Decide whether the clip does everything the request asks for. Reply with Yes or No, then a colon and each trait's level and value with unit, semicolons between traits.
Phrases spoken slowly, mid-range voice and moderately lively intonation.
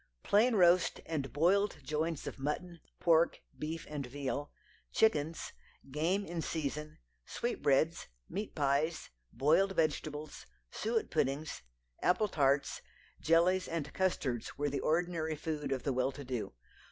Yes: slow, 130 wpm; medium, 155 Hz; average, 3.4 semitones